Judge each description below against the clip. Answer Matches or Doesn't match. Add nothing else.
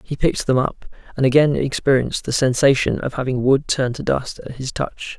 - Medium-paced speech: Doesn't match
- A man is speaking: Matches